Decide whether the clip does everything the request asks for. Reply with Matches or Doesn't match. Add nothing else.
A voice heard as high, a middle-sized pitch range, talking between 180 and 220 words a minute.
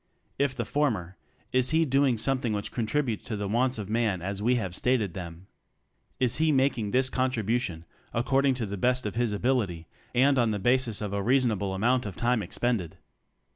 Doesn't match